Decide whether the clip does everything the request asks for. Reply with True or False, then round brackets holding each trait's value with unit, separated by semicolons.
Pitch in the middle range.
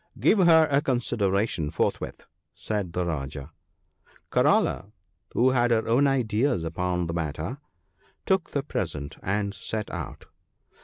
False (105 Hz)